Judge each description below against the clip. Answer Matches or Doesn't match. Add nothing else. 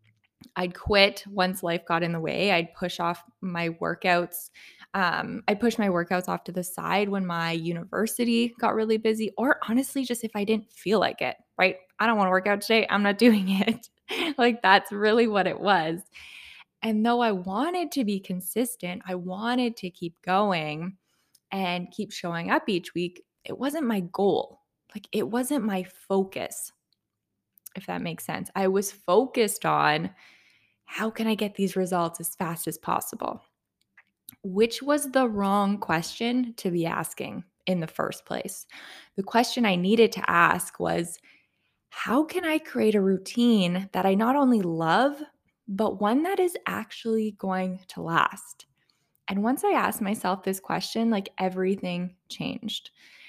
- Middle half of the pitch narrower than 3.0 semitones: Doesn't match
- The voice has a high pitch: Matches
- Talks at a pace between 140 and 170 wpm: Matches